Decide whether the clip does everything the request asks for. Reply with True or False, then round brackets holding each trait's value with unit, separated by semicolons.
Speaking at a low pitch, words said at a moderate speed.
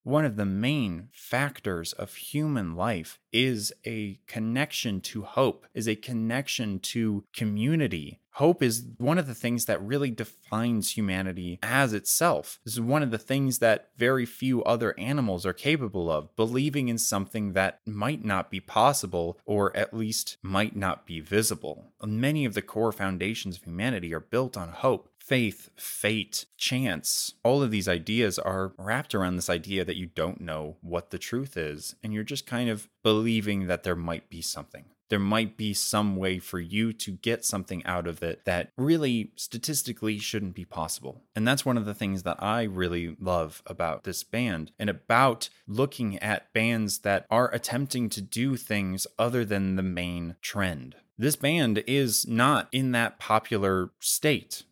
True (110 Hz; 170 wpm)